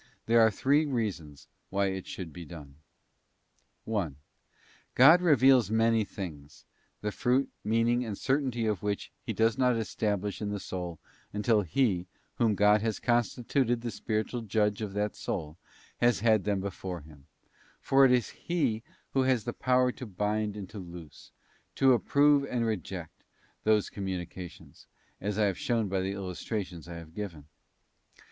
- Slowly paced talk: No, average, 160 wpm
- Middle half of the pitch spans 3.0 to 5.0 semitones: Yes, average, 4.2 semitones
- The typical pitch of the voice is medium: No, low, 105 Hz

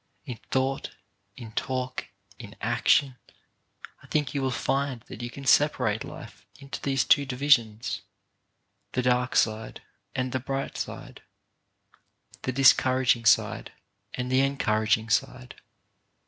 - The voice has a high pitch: No, low, 130 Hz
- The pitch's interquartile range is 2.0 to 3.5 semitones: Yes, narrow, 2.4 semitones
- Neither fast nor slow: No, slow, 130 wpm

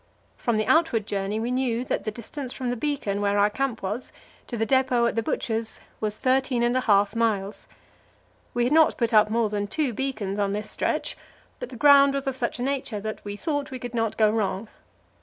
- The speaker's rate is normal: No, fast, 220 wpm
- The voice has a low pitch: No, high, 230 Hz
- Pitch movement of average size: Yes, average, 3.8 semitones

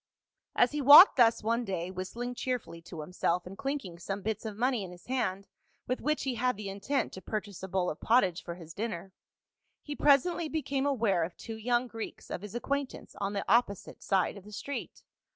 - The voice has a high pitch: Yes, high, 220 Hz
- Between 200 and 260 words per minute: Yes, fast, 205 wpm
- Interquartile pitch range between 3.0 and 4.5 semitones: No, average, 5.2 semitones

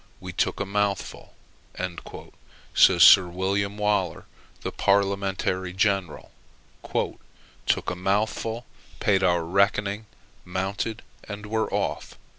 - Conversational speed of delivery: No, slow, 100 wpm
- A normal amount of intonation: No, narrow, 1.8 semitones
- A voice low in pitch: Yes, low, 100 Hz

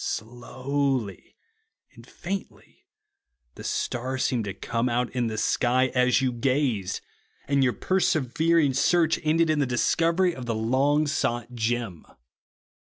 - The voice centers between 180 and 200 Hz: No, low, 130 Hz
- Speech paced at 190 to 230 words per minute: No, slow, 135 wpm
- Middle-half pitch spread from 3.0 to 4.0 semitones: Yes, average, 3.5 semitones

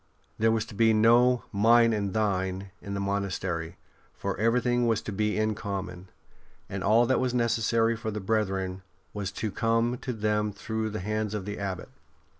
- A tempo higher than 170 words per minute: Yes, average, 190 wpm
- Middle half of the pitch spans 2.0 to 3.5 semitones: Yes, narrow, 2.6 semitones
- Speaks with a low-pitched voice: Yes, low, 110 Hz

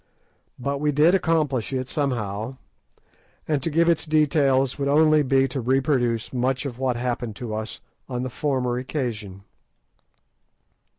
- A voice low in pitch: Yes, low, 130 Hz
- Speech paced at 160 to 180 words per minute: No, average, 140 wpm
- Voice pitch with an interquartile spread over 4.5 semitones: No, average, 3.3 semitones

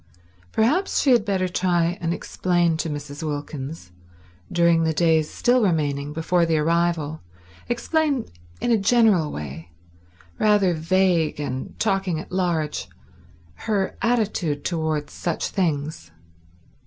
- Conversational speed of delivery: No, slow, 115 wpm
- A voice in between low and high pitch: Yes, medium, 170 Hz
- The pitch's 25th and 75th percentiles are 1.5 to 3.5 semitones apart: No, average, 4.4 semitones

